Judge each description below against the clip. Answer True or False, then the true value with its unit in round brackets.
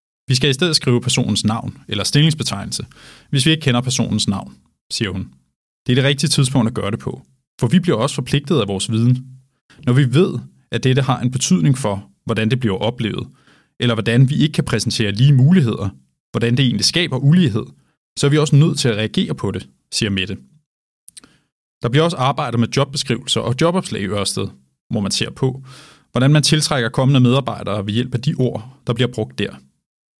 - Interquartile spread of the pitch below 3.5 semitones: False (4.3 semitones)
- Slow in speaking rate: False (200 wpm)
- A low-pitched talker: True (125 Hz)